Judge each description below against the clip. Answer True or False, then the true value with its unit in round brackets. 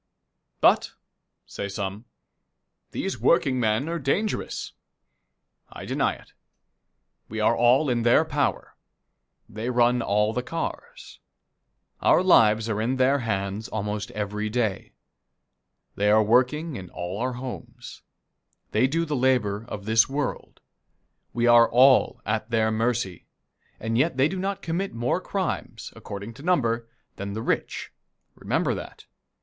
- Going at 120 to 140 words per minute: True (135 wpm)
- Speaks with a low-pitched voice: True (120 Hz)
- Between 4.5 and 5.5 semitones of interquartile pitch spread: False (3.7 semitones)